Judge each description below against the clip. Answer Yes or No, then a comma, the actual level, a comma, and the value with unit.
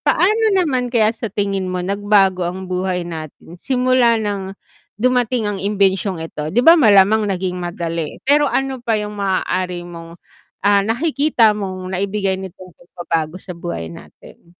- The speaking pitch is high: Yes, high, 195 Hz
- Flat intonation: No, average, 3.9 semitones